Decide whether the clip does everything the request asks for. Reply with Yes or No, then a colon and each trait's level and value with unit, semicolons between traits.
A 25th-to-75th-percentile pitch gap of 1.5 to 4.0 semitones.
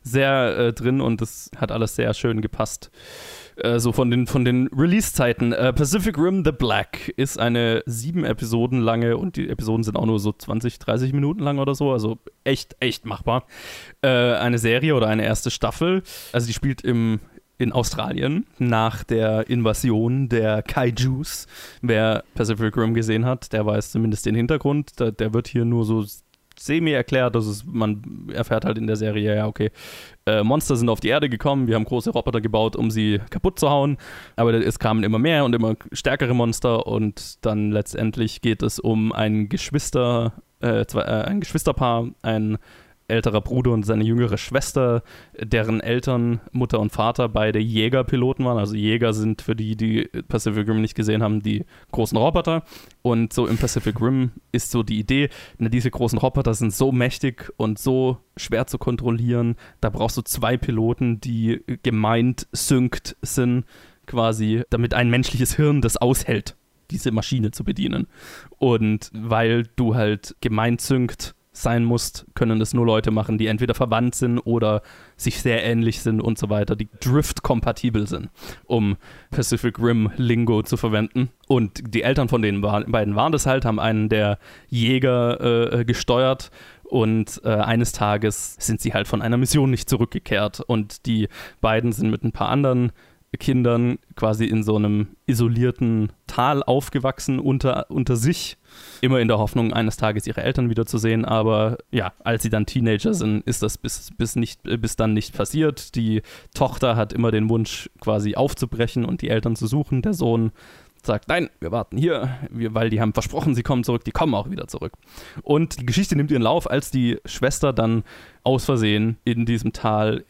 Yes: average, 2.7 semitones